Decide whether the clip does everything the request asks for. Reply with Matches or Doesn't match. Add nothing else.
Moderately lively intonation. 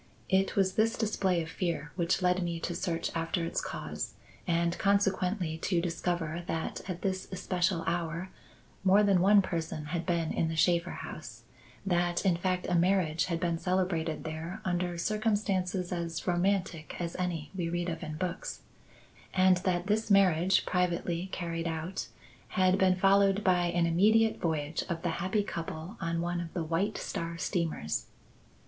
Doesn't match